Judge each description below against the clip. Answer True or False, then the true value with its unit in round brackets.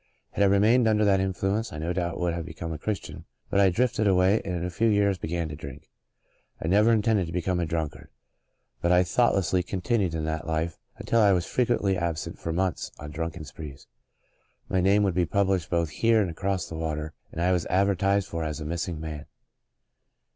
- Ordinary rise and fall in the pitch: True (3.4 semitones)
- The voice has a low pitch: True (90 Hz)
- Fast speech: True (210 wpm)